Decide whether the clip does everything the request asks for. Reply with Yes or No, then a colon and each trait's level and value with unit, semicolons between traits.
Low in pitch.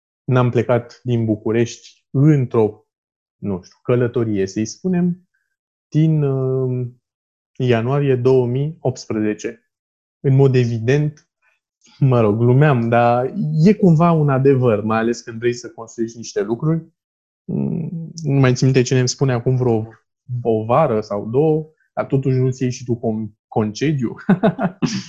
Yes: low, 125 Hz